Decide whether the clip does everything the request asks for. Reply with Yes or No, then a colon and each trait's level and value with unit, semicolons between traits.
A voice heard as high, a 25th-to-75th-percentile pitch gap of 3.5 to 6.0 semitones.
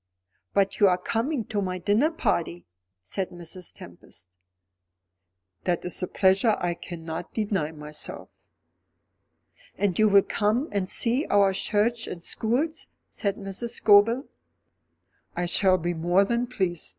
Yes: high, 195 Hz; average, 4.2 semitones